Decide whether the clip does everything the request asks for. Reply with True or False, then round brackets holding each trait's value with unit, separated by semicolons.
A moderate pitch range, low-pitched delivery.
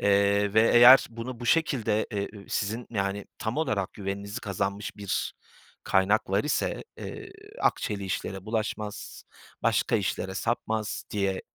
False (2.3 semitones; 105 Hz)